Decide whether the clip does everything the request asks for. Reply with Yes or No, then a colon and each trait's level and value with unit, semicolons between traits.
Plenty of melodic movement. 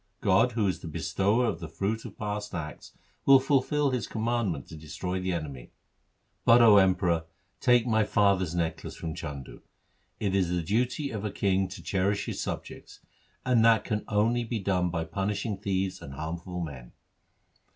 No: average, 4.5 semitones